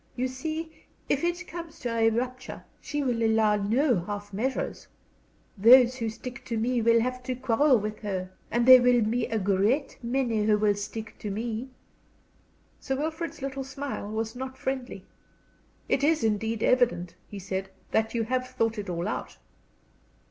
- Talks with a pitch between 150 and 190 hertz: No, high, 235 Hz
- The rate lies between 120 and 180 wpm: Yes, average, 170 wpm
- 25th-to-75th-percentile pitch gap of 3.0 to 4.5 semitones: Yes, average, 3.3 semitones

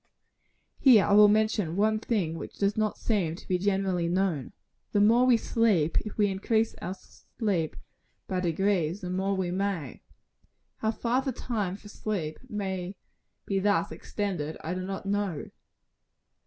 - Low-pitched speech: No, high, 195 Hz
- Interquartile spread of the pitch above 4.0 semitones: No, average, 3.0 semitones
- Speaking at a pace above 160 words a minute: No, average, 155 wpm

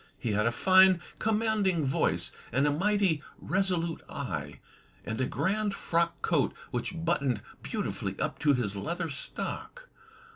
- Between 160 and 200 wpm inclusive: No, average, 140 wpm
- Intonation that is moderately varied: No, wide, 6.4 semitones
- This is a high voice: No, medium, 165 Hz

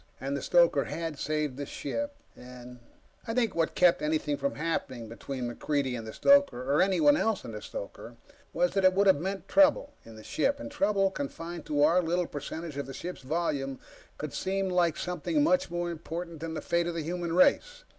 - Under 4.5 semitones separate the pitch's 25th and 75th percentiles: No, average, 5.2 semitones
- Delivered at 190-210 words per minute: Yes, average, 200 wpm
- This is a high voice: No, medium, 170 Hz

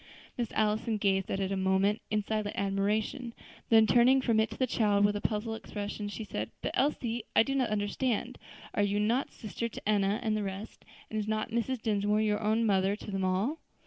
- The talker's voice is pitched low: No, high, 215 Hz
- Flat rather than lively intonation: Yes, narrow, 1.9 semitones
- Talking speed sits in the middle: No, fast, 210 wpm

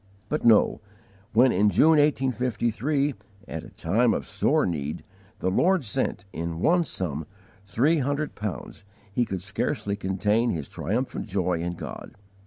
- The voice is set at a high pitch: No, low, 105 Hz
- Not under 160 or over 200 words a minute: No, average, 145 wpm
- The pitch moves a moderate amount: No, wide, 6.5 semitones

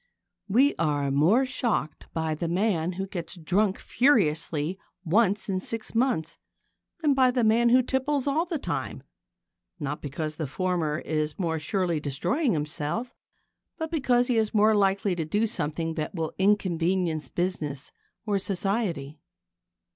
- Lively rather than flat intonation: Yes, wide, 6.3 semitones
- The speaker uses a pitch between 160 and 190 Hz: Yes, medium, 185 Hz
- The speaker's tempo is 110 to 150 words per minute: Yes, average, 145 wpm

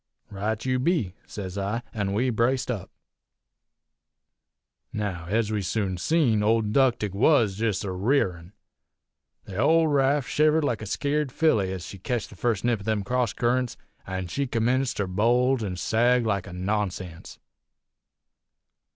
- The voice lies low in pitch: Yes, low, 110 Hz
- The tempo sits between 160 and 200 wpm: No, average, 150 wpm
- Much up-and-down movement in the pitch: No, average, 4.5 semitones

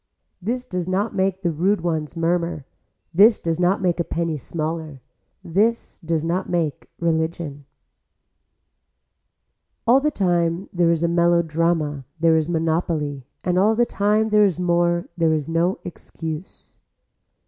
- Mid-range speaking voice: Yes, medium, 170 Hz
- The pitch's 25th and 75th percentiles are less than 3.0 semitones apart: Yes, narrow, 2.5 semitones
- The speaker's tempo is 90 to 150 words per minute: Yes, average, 140 wpm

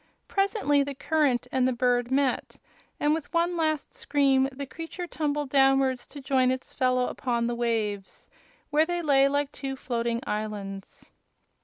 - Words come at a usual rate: Yes, average, 155 wpm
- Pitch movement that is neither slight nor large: Yes, average, 3.2 semitones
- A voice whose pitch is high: Yes, very high, 270 Hz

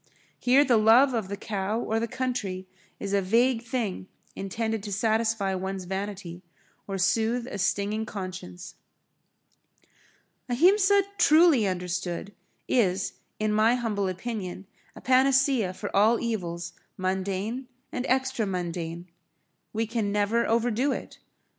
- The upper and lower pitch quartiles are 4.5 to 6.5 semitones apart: No, average, 3.9 semitones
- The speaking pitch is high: Yes, high, 215 Hz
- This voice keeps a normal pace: No, slow, 125 wpm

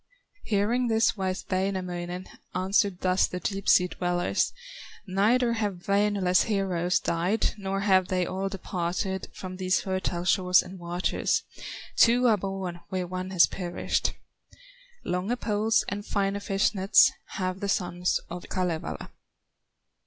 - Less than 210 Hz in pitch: Yes, high, 190 Hz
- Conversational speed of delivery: No, slow, 130 wpm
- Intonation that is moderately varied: No, narrow, 1.9 semitones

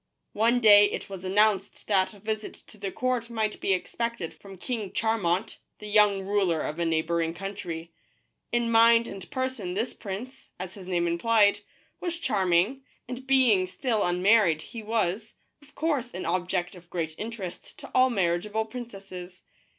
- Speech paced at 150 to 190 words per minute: Yes, average, 165 wpm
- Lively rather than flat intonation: No, average, 4.2 semitones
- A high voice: Yes, high, 205 Hz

